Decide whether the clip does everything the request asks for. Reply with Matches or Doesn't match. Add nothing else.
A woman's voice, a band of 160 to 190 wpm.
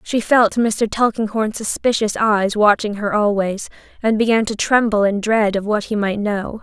Matches